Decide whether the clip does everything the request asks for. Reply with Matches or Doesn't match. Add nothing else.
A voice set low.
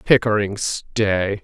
Matches